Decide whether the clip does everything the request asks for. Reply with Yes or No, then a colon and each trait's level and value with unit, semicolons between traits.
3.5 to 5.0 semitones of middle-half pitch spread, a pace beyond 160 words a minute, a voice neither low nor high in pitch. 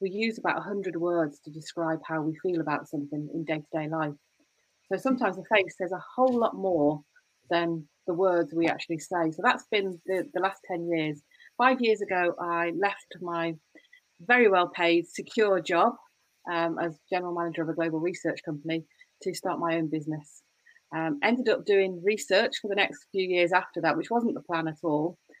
No: average, 3.1 semitones; average, 195 wpm; medium, 175 Hz